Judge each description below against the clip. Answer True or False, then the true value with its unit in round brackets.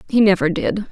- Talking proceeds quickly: False (195 wpm)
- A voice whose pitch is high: True (195 Hz)